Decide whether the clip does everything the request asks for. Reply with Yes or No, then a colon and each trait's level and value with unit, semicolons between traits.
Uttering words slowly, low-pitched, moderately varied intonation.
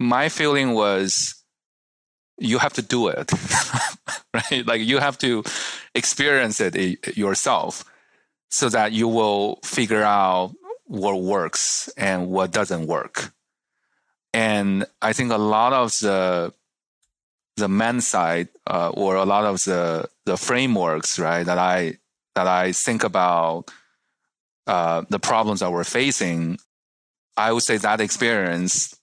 Yes: slow, 130 wpm; low, 100 Hz; average, 3.7 semitones